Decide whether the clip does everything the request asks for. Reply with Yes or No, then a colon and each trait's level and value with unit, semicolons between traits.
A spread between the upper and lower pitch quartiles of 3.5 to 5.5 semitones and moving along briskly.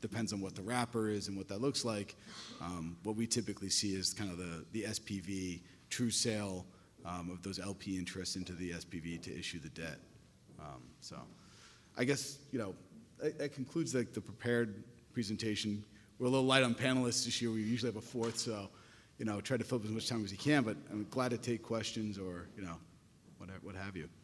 Yes: average, 3.8 semitones; fast, 220 wpm